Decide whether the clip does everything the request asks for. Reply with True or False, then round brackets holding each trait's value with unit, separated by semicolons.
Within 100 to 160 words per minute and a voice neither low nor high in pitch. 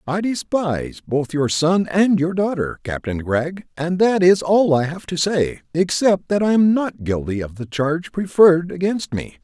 False (190 wpm; 170 Hz)